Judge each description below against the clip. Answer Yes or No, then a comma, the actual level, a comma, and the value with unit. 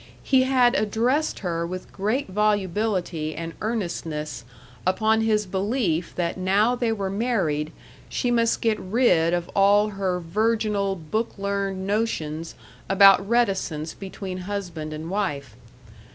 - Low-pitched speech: No, high, 195 Hz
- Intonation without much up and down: No, average, 4.3 semitones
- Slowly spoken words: Yes, slow, 125 wpm